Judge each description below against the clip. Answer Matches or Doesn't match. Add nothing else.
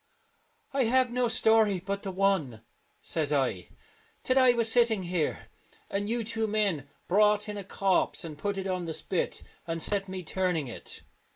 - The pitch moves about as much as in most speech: Matches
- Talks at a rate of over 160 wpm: Matches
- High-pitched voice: Matches